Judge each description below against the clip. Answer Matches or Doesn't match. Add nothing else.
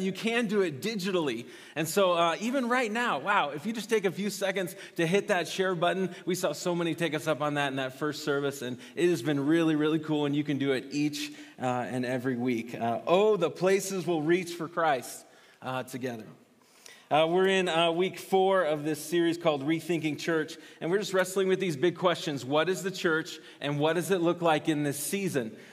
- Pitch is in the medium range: Matches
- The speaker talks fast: Matches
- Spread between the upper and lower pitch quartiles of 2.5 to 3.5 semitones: Doesn't match